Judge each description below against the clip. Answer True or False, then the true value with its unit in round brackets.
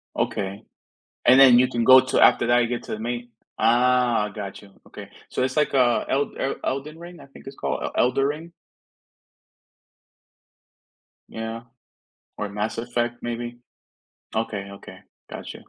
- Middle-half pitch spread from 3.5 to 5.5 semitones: False (2.5 semitones)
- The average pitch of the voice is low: True (120 Hz)